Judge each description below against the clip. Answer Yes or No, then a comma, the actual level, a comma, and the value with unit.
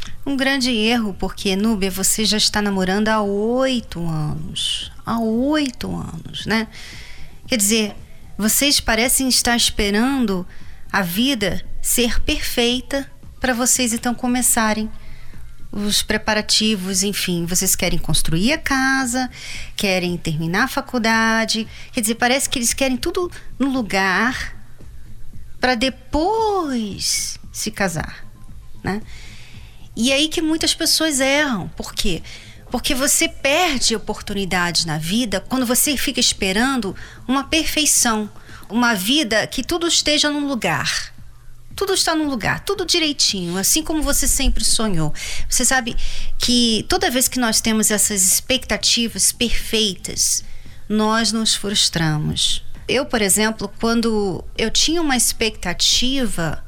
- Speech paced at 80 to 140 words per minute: Yes, average, 125 wpm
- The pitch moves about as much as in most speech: Yes, average, 4.6 semitones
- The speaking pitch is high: Yes, high, 235 Hz